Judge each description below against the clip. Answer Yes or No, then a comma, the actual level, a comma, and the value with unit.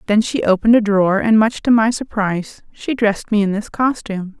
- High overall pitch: Yes, high, 215 Hz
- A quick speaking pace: Yes, fast, 220 wpm